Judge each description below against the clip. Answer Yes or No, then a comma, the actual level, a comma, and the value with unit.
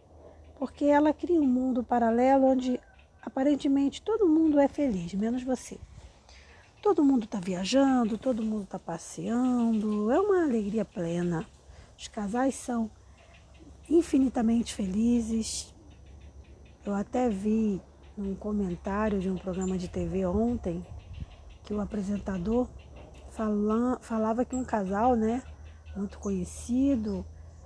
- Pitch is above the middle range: Yes, high, 220 Hz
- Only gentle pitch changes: No, average, 5.1 semitones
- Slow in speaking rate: Yes, slow, 115 wpm